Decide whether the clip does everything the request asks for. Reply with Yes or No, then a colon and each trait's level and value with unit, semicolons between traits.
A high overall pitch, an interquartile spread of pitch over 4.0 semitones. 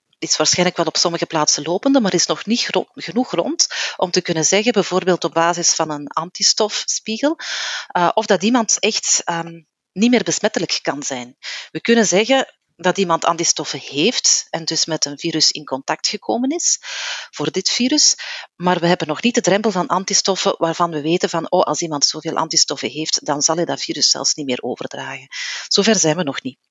No: medium, 175 Hz; average, 4.8 semitones